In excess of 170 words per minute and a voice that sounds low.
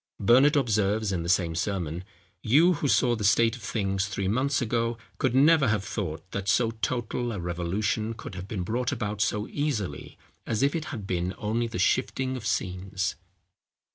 Yes: average, 180 wpm; low, 110 Hz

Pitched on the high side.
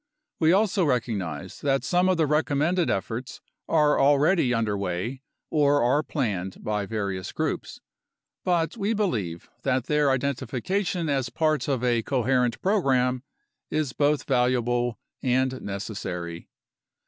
No: low, 130 Hz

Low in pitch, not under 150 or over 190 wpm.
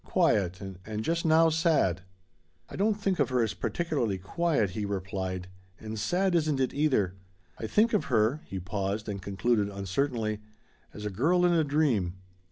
Yes: low, 110 Hz; average, 170 wpm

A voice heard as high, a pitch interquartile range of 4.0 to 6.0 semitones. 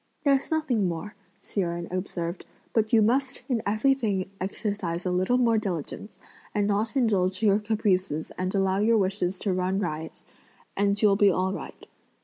No: high, 200 Hz; average, 3.1 semitones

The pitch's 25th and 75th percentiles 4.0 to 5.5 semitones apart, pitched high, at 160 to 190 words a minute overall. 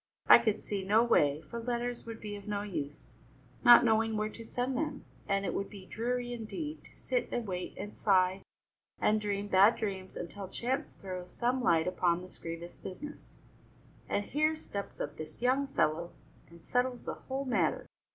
Yes: average, 4.7 semitones; high, 210 Hz; average, 180 wpm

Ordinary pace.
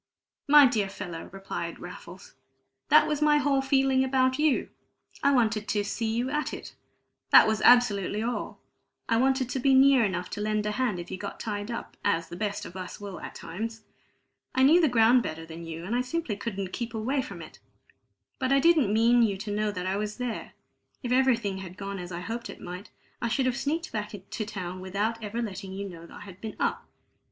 No: fast, 215 wpm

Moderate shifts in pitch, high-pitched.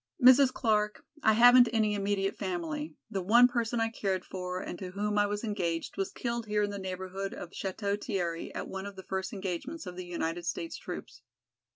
Yes: average, 3.1 semitones; high, 195 Hz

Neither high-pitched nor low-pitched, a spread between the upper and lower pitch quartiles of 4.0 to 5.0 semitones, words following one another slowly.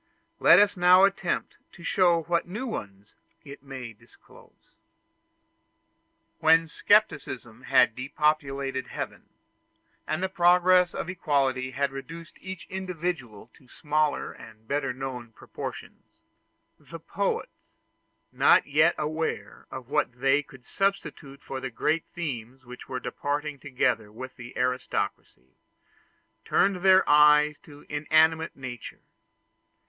Yes: medium, 145 Hz; average, 4.7 semitones; slow, 120 wpm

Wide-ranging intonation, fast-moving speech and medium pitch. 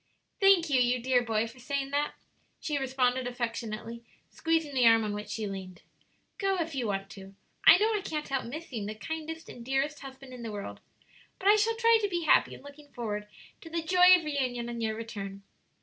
No: wide, 5.8 semitones; fast, 210 wpm; very high, 260 Hz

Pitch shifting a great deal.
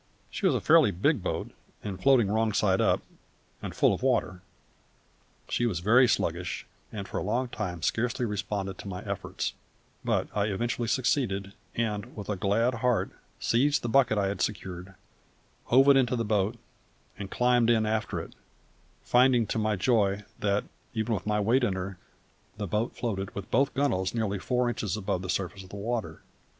No: average, 3.5 semitones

